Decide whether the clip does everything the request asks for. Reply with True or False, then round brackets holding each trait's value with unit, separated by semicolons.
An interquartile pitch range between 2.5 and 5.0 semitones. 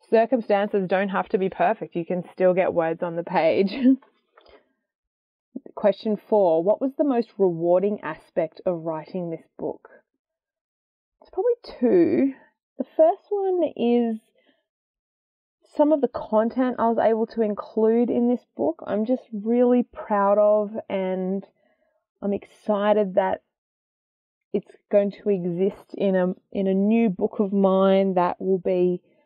True (4.7 semitones)